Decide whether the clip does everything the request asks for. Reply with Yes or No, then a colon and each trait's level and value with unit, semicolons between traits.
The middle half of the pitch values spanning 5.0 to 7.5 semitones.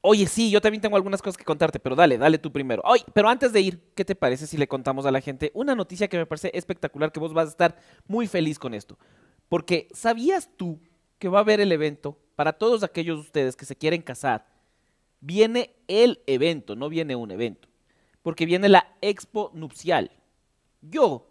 Yes: average, 5.3 semitones